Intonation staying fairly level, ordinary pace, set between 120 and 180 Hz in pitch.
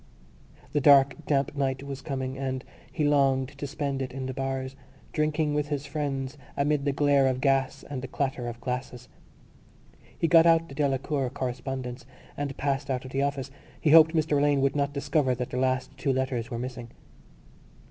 Yes: narrow, 1.7 semitones; average, 185 wpm; low, 135 Hz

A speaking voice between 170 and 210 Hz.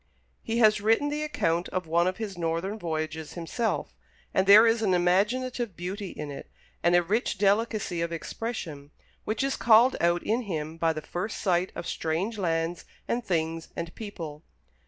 Yes: medium, 185 Hz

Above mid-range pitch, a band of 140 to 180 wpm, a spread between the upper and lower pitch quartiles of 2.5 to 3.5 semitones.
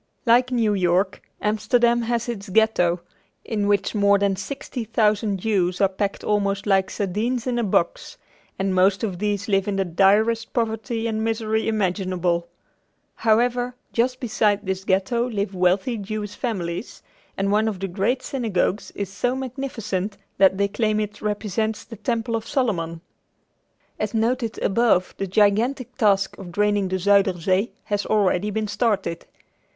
Yes: high, 210 Hz; average, 155 wpm; average, 2.9 semitones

